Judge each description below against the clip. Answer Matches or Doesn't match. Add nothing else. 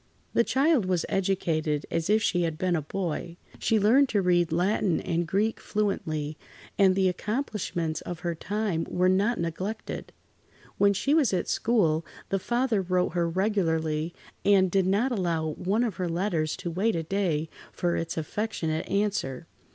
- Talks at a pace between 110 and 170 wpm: Matches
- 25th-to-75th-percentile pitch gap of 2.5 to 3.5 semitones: Doesn't match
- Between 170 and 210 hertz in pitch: Matches